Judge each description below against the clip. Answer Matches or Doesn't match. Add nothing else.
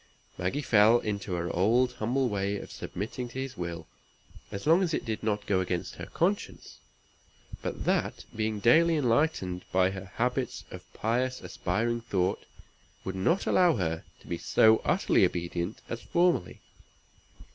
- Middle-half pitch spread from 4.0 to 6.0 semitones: Matches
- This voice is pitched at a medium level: Doesn't match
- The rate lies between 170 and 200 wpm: Doesn't match